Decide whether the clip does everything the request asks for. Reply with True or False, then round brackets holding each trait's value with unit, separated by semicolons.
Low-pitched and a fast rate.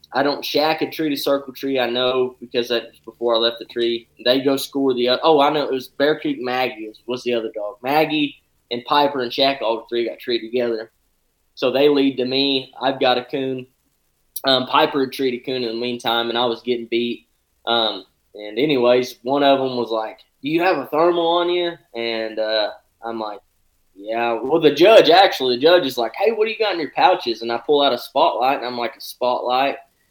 True (125 Hz; 225 wpm)